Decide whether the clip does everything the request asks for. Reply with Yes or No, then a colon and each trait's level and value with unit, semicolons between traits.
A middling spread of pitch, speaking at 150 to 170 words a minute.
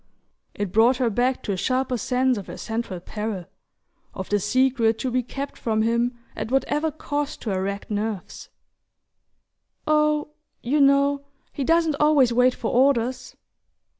Yes: average, 4.0 semitones; average, 155 wpm